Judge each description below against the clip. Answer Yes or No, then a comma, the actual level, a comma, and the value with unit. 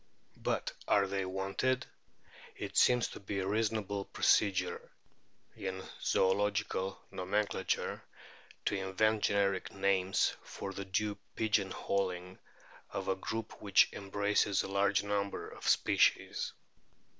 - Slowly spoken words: Yes, slow, 120 wpm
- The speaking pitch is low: Yes, low, 100 Hz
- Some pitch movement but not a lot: No, narrow, 1.3 semitones